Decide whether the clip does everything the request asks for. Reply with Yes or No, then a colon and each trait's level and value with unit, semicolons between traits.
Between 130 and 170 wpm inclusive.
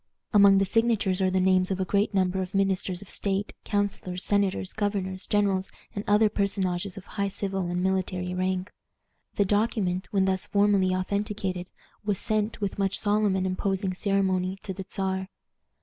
Yes: average, 165 wpm